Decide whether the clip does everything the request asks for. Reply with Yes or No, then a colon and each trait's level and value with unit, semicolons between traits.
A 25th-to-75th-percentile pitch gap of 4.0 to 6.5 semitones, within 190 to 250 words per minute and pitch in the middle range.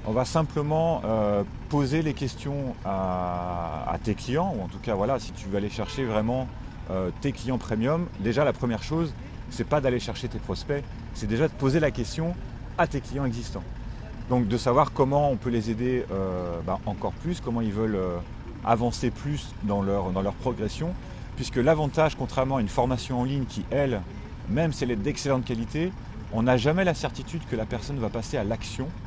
No: average, 4.6 semitones; average, 200 wpm; low, 120 Hz